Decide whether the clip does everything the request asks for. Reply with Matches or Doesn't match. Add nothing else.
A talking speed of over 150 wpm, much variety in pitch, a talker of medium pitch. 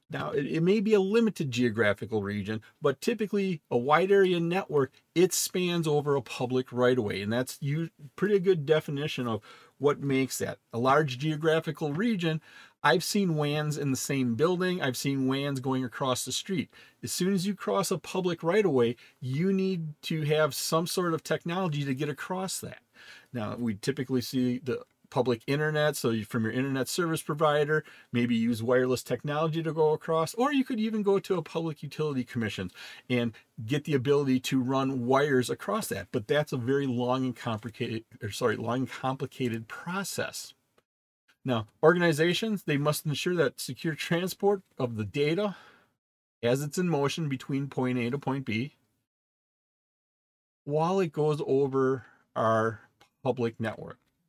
Doesn't match